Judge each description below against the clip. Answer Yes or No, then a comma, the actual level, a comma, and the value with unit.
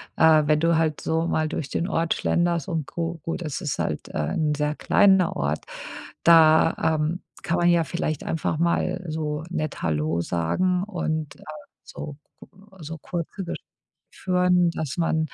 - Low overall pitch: No, medium, 160 Hz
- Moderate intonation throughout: No, narrow, 2.1 semitones